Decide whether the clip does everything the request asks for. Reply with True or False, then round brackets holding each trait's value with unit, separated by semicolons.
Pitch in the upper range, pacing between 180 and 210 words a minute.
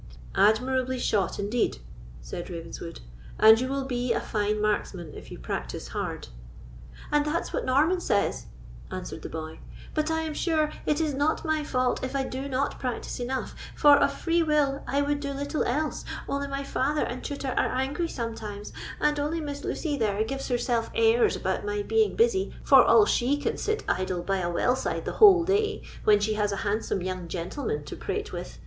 True (260 Hz; 190 wpm)